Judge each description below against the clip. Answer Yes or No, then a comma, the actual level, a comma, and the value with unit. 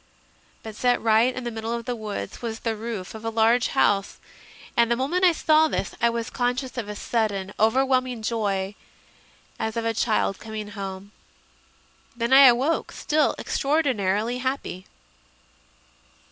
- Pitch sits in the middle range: No, high, 230 Hz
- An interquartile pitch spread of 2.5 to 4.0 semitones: Yes, average, 2.9 semitones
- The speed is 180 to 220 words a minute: No, average, 160 wpm